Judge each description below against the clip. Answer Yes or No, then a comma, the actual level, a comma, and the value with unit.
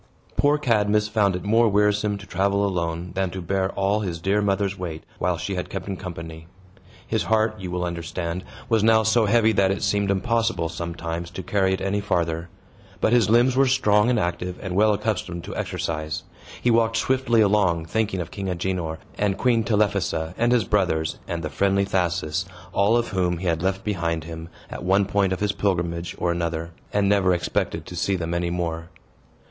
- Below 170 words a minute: No, average, 195 wpm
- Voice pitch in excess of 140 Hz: No, very low, 95 Hz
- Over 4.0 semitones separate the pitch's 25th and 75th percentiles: No, average, 3.4 semitones